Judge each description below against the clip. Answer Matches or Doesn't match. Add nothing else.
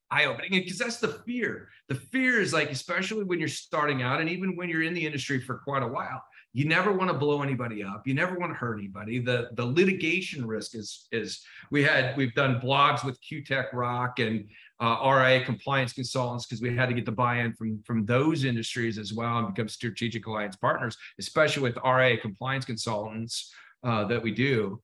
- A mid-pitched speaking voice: Doesn't match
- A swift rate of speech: Matches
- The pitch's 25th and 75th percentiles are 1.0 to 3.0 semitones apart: Doesn't match